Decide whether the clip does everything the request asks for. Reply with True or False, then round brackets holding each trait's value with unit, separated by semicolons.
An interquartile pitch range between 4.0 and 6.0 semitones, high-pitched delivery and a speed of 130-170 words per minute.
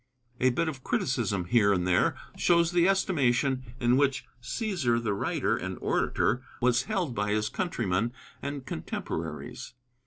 False (5.3 semitones; 125 Hz; 145 wpm)